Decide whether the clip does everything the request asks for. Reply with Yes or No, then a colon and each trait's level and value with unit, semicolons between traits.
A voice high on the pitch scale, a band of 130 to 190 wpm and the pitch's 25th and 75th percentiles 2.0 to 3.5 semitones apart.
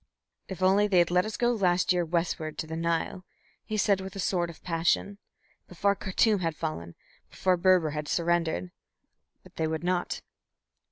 No: medium, 175 Hz; average, 175 wpm; average, 2.7 semitones